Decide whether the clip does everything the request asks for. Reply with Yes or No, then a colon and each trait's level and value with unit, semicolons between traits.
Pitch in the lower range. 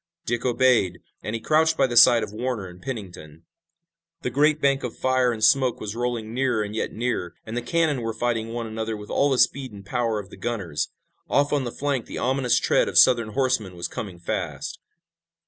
Yes: low, 120 Hz